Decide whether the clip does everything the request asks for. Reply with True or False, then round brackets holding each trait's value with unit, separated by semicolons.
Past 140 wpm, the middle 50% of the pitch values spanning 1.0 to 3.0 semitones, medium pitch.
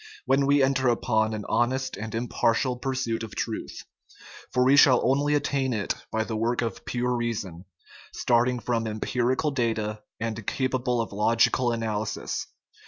False (155 wpm; 2.6 semitones; 120 Hz)